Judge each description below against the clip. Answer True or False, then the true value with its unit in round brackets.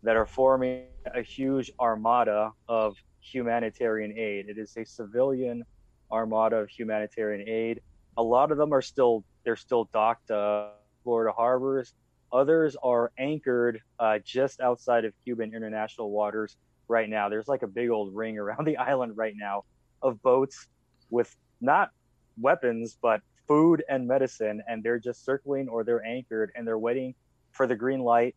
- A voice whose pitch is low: True (115 Hz)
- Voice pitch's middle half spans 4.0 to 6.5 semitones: False (2.7 semitones)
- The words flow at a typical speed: True (160 wpm)